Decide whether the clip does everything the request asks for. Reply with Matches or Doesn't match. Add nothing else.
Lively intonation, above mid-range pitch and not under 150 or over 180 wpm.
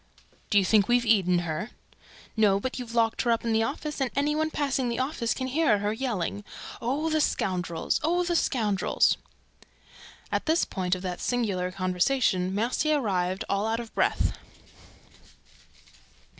Matches